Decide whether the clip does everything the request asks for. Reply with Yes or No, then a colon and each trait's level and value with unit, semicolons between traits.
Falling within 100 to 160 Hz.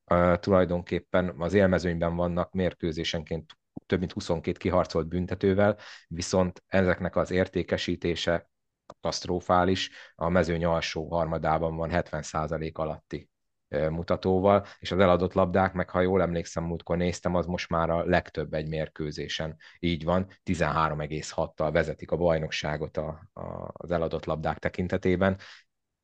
No: very low, 85 Hz